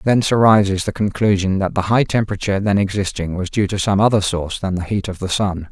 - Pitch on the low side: Yes, low, 100 Hz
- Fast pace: Yes, fast, 230 wpm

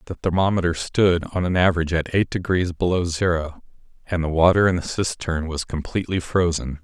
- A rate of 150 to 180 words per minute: Yes, average, 175 wpm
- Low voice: Yes, very low, 85 Hz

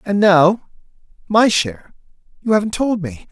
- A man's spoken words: Yes, male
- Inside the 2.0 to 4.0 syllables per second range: No, 4.6 syllables/s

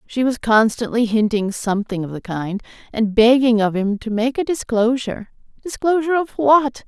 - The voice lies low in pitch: No, high, 235 Hz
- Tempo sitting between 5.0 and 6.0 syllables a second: Yes, 5.1 syllables/s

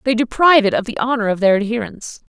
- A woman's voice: Yes, female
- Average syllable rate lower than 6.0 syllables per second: No, 7.2 syllables/s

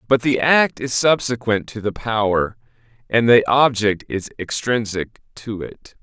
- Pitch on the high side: No, low, 115 Hz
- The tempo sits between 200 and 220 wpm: No, average, 150 wpm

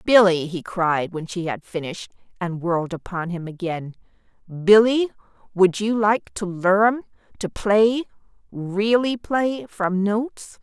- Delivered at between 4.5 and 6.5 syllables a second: No, 4.0 syllables/s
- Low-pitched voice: No, high, 195 Hz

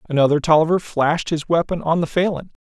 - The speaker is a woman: No, male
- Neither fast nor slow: Yes, average, 185 wpm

